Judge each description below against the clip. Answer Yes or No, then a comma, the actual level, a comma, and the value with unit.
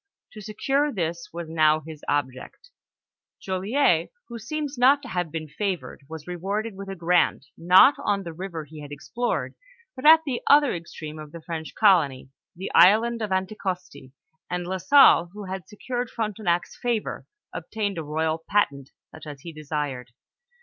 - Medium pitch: Yes, medium, 180 Hz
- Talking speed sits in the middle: Yes, average, 165 wpm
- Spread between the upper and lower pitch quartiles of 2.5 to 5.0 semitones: No, wide, 5.4 semitones